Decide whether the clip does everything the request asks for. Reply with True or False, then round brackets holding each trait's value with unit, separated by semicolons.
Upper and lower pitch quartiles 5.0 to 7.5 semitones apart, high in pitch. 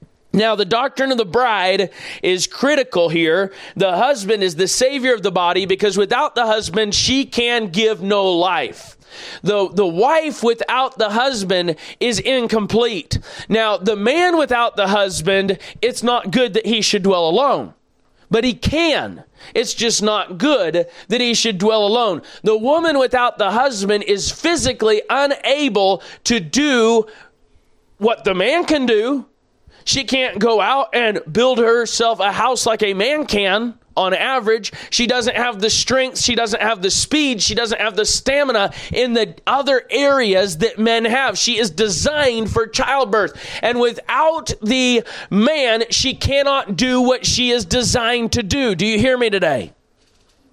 False (3.7 semitones; 230 Hz)